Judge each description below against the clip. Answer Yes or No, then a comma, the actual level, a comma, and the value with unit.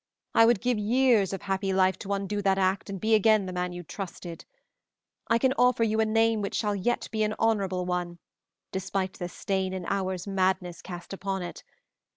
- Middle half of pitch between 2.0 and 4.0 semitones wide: Yes, narrow, 2.6 semitones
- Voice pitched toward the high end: Yes, high, 195 Hz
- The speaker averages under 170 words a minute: No, average, 195 wpm